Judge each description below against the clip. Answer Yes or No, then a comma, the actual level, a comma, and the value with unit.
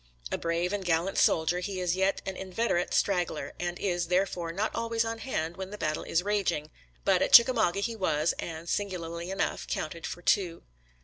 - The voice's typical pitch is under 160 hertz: No, medium, 180 Hz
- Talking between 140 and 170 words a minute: No, average, 185 wpm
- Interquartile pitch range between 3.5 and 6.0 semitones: No, average, 3.0 semitones